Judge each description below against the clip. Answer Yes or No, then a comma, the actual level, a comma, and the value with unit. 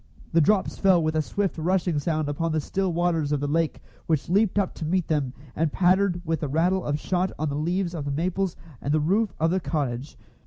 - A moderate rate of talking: No, fast, 230 wpm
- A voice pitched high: No, medium, 165 Hz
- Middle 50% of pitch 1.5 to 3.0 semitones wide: No, average, 3.5 semitones